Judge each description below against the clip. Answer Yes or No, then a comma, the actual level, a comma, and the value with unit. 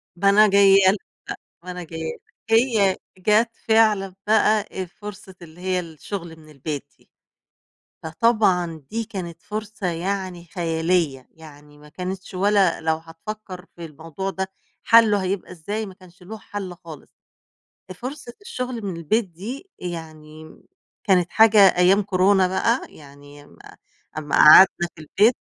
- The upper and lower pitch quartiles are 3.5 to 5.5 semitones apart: Yes, average, 4.0 semitones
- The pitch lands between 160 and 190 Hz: Yes, medium, 185 Hz